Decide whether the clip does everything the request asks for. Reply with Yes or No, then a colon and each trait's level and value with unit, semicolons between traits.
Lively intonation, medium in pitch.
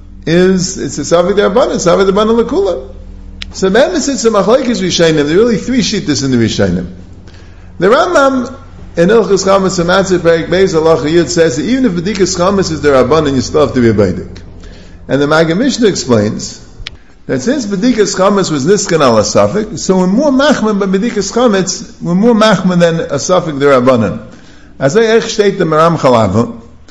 Yes: wide, 7.4 semitones; medium, 175 Hz